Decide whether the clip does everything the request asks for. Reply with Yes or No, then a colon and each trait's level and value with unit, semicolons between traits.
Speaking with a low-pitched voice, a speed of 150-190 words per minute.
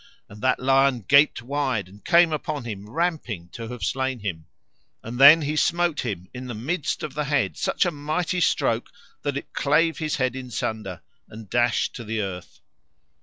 Yes: low, 130 Hz; average, 185 wpm